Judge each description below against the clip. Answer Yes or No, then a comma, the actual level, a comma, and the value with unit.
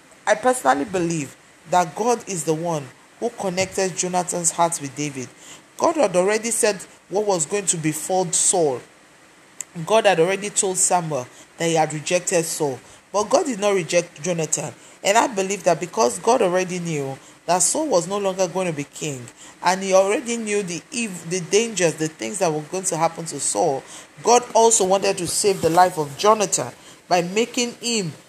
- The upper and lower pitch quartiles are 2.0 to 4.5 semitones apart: Yes, average, 3.9 semitones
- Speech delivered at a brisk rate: No, average, 180 wpm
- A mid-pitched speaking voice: Yes, medium, 180 Hz